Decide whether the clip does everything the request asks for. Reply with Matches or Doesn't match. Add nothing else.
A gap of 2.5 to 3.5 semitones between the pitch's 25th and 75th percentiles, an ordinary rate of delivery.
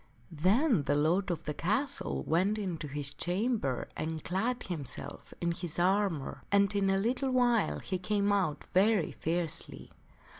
Doesn't match